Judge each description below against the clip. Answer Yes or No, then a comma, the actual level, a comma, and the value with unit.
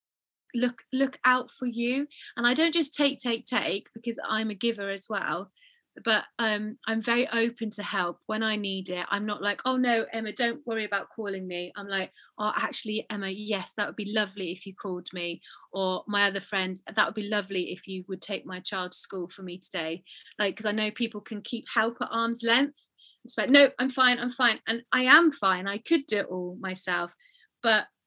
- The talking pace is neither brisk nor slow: No, fast, 220 wpm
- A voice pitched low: No, high, 215 Hz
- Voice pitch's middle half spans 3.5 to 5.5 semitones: Yes, average, 3.8 semitones